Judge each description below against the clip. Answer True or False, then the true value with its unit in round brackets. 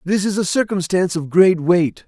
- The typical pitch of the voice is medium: True (180 Hz)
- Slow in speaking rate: False (205 wpm)